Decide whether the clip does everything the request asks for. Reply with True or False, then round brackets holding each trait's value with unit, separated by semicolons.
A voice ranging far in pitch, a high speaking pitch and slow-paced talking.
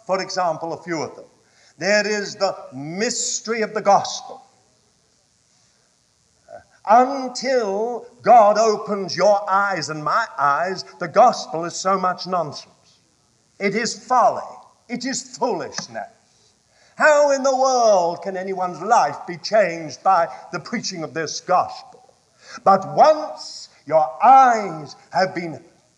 True (5.9 semitones; 200 Hz; 125 wpm)